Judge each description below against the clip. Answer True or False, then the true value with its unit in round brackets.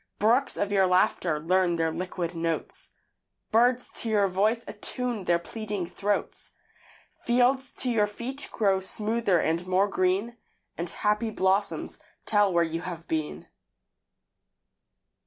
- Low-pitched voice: False (195 Hz)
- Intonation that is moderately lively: True (4.2 semitones)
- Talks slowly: True (130 wpm)